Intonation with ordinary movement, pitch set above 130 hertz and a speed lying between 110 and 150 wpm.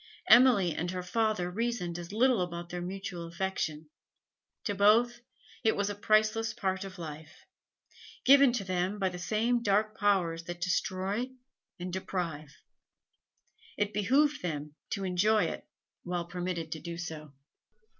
Yes: average, 3.7 semitones; high, 190 Hz; average, 145 wpm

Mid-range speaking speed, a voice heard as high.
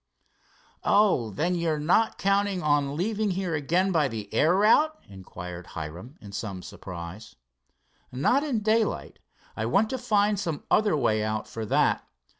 No: average, 150 wpm; medium, 160 Hz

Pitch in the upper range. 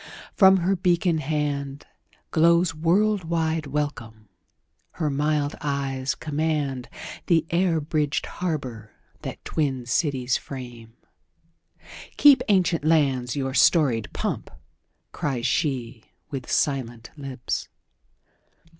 No: medium, 145 Hz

